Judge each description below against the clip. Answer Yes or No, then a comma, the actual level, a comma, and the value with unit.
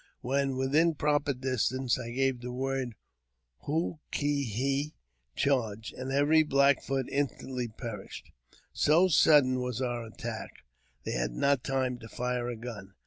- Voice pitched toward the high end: No, low, 130 Hz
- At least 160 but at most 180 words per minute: No, average, 140 wpm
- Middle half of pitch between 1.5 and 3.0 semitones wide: Yes, narrow, 2.6 semitones